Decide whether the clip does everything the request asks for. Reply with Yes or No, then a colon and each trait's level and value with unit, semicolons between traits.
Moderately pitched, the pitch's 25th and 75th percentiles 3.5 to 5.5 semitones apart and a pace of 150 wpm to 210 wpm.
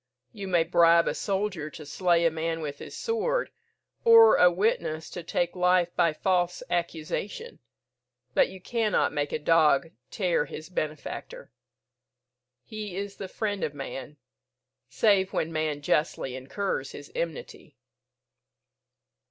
No: medium, 175 Hz; average, 4.3 semitones; slow, 135 wpm